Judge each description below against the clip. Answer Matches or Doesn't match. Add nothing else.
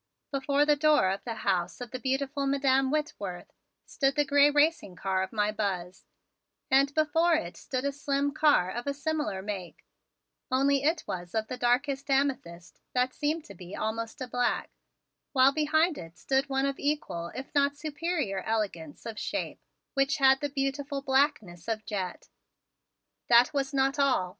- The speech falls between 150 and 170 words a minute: Matches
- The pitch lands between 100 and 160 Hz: Doesn't match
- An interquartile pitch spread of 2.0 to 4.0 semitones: Doesn't match